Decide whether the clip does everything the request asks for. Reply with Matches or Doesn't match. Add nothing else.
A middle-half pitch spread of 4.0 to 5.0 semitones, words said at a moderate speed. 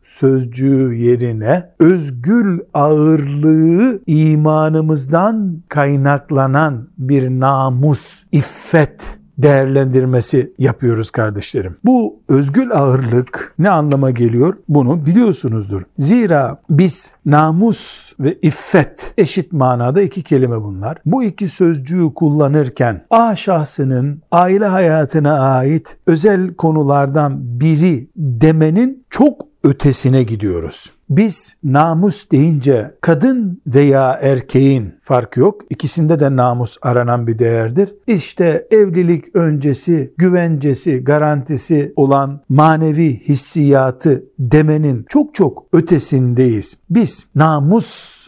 Doesn't match